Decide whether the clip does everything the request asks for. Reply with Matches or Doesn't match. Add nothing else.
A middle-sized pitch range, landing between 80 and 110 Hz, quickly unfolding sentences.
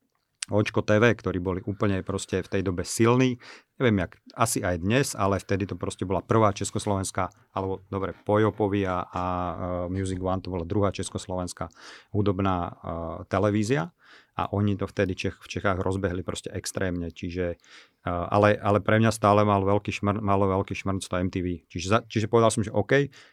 Doesn't match